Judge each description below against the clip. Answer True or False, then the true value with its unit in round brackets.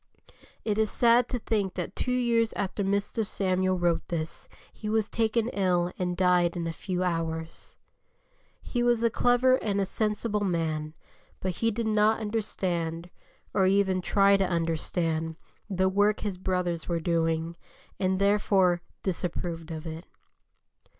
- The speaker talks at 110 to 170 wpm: True (150 wpm)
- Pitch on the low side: False (190 Hz)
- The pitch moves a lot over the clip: False (3.7 semitones)